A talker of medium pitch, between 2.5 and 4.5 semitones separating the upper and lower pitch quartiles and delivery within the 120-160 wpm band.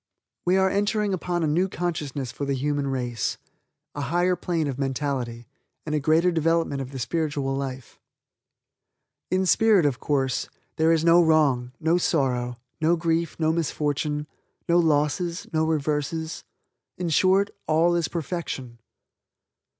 Yes: medium, 155 Hz; average, 3.6 semitones; average, 140 wpm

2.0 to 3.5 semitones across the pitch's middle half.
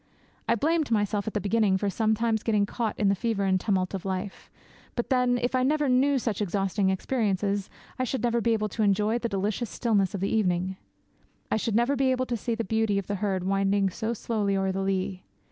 Yes: average, 3.2 semitones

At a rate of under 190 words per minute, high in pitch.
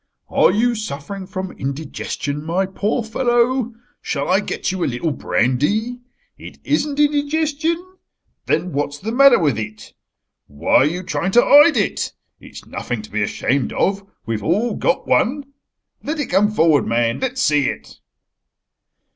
Yes: average, 155 wpm; high, 195 Hz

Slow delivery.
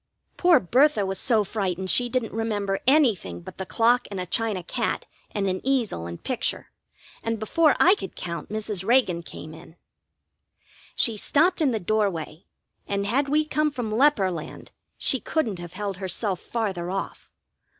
No: average, 165 wpm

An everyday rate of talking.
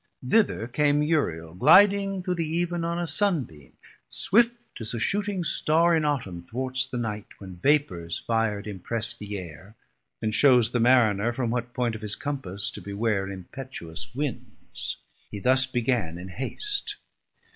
Yes: average, 155 wpm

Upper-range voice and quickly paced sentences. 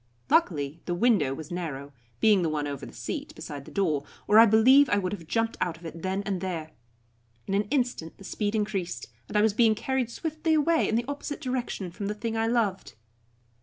Yes: high, 205 Hz; fast, 215 wpm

